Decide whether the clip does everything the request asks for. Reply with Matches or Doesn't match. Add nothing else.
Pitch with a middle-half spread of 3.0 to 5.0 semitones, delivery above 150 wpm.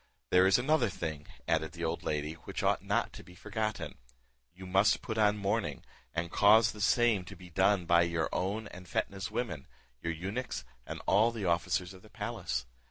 Matches